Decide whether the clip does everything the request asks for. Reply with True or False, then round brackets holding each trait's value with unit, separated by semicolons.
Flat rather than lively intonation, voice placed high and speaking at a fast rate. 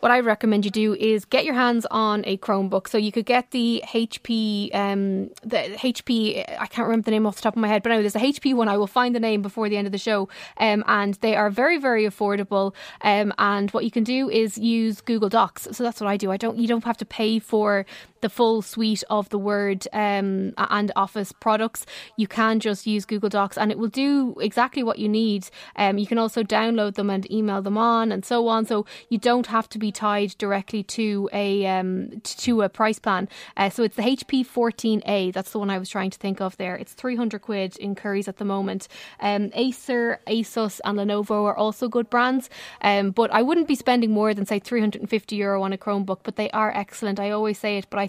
True (2.1 semitones; 215 Hz; 240 wpm)